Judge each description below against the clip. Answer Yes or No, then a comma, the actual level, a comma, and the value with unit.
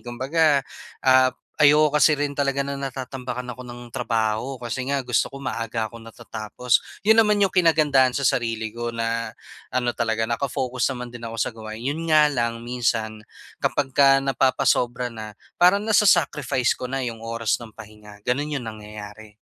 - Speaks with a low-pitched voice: Yes, low, 125 Hz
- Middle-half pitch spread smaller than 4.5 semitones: Yes, average, 3.3 semitones